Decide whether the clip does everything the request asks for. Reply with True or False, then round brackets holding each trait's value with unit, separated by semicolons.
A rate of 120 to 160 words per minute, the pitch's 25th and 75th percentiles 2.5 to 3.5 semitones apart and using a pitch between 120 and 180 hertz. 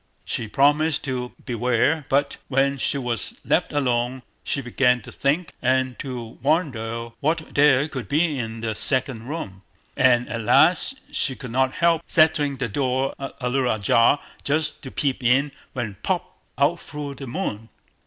True (155 wpm; 3.2 semitones; 135 Hz)